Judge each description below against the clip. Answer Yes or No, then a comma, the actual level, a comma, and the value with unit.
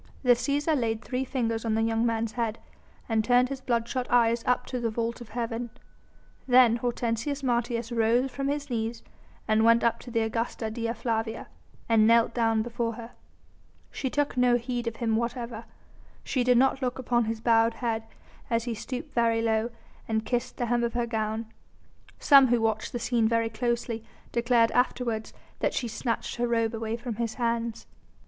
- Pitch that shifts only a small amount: Yes, narrow, 1.4 semitones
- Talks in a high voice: Yes, high, 235 Hz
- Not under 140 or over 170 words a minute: No, average, 185 wpm